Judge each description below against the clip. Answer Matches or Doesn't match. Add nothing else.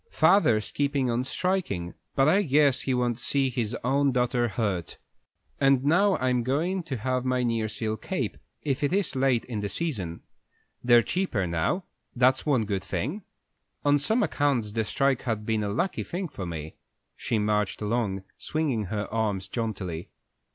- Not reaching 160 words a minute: Doesn't match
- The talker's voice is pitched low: Matches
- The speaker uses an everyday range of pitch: Matches